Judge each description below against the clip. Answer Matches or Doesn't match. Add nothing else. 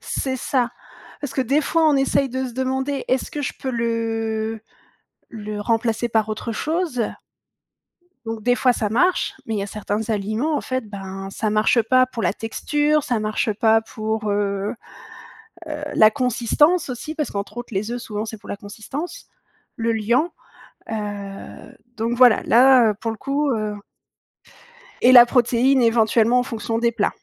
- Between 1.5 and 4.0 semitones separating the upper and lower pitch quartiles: Matches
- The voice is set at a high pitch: Matches